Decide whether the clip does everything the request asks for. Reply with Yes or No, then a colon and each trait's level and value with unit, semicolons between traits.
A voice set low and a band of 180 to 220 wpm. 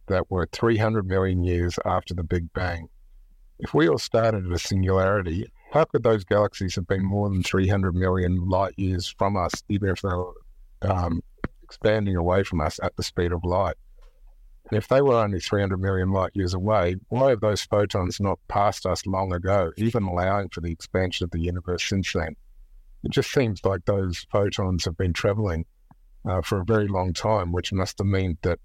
Yes: very low, 95 Hz; average, 195 wpm